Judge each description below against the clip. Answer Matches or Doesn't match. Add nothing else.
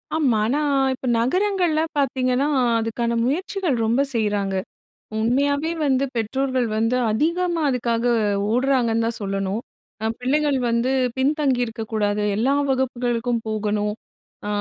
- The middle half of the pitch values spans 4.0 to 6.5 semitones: Doesn't match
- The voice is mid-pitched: Doesn't match